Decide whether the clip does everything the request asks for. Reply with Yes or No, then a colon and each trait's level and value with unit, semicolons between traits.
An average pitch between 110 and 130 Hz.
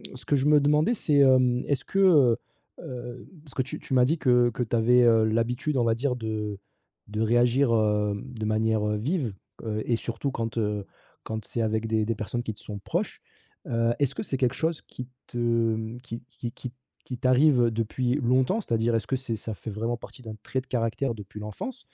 Yes: low, 120 Hz